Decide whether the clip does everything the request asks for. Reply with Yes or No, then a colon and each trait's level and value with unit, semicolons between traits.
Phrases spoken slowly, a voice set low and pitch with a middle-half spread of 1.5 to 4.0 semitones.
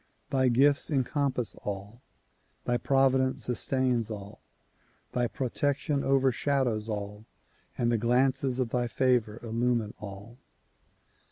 Yes: slow, 105 wpm; low, 125 Hz; average, 2.9 semitones